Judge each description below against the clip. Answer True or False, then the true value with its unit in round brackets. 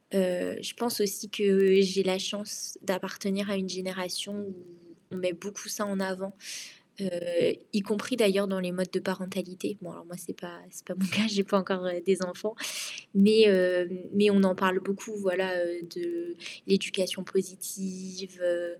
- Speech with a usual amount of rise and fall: False (1.5 semitones)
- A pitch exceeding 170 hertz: True (190 Hz)